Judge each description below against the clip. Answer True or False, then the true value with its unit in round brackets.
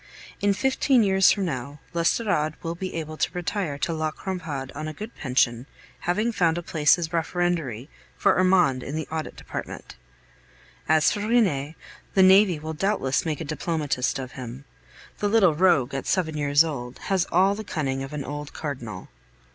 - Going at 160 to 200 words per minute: True (175 wpm)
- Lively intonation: False (4.8 semitones)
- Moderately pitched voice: True (160 Hz)